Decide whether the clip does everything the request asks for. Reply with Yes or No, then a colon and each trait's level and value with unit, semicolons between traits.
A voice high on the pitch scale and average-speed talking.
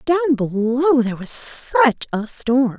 Yes: very high, 255 Hz; average, 150 wpm